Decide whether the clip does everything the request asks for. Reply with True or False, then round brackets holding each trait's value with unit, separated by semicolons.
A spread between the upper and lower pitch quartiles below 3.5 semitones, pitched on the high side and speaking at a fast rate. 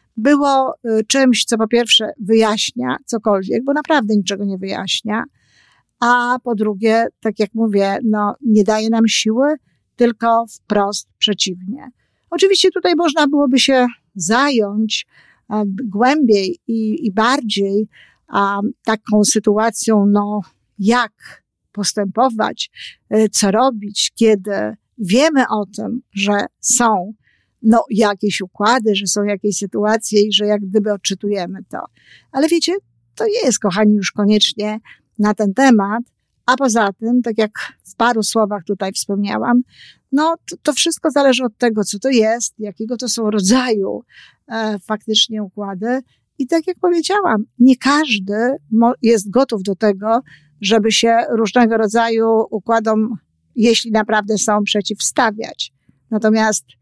False (2.9 semitones; 220 Hz; 130 wpm)